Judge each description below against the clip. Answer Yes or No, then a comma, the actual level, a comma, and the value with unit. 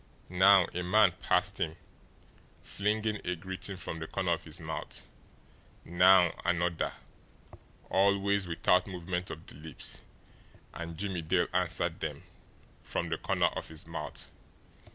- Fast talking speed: No, slow, 135 wpm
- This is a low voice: Yes, very low, 90 Hz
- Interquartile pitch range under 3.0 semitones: Yes, narrow, 2.6 semitones